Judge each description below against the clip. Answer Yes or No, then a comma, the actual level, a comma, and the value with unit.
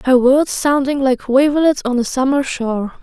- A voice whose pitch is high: Yes, very high, 265 Hz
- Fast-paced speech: No, average, 180 wpm